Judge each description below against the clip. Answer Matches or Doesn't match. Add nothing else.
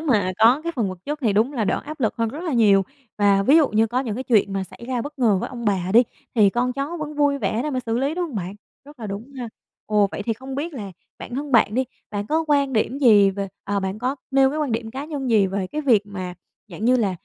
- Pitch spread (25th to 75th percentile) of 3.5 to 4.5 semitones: Doesn't match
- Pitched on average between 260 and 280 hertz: Doesn't match